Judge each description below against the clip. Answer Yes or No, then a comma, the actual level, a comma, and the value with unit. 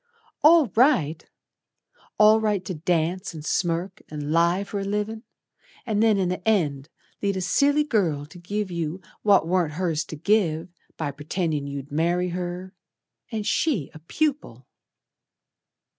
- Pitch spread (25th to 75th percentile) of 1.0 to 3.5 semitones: No, average, 4.7 semitones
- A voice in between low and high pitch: Yes, medium, 180 Hz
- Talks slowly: No, average, 145 wpm